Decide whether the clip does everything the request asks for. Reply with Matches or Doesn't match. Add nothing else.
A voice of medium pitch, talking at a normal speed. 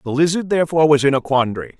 Doesn't match